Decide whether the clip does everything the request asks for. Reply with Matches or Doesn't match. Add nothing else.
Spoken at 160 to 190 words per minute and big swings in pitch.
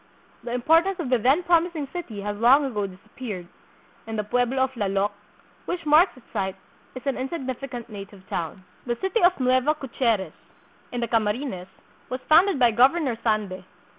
Matches